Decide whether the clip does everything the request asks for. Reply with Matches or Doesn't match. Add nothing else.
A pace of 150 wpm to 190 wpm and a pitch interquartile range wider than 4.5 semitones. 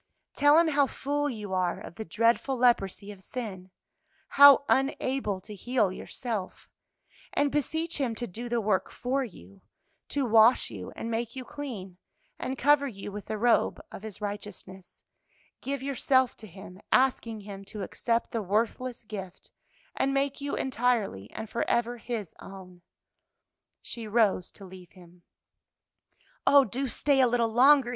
Matches